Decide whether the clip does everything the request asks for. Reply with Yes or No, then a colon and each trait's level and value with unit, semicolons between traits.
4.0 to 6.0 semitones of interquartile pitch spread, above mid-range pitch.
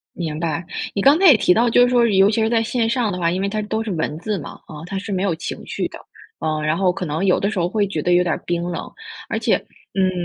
Yes: average, 4.3 semitones; high, 195 Hz